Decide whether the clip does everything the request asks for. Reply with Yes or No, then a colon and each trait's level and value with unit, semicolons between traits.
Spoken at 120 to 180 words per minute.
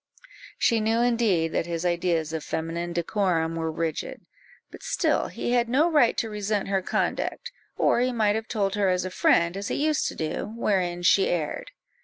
No: average, 190 wpm